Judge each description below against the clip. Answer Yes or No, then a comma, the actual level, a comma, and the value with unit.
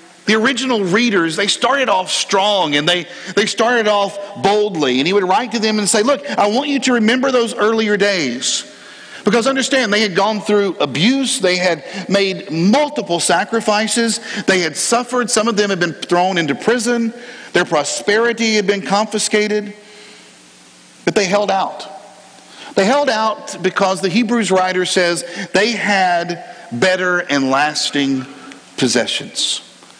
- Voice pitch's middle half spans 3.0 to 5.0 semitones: Yes, average, 4.0 semitones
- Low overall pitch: No, high, 205 Hz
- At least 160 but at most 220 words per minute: No, average, 150 wpm